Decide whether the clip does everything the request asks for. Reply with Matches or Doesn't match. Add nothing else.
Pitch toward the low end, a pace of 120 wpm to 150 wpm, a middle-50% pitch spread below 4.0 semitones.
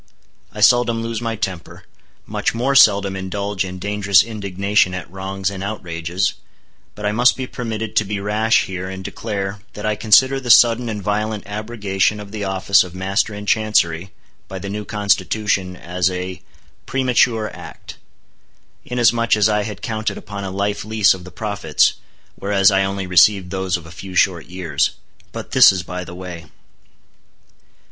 Doesn't match